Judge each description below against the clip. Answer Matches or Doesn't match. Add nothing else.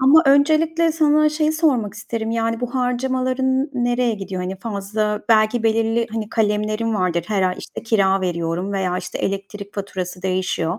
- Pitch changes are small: Doesn't match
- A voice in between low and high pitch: Doesn't match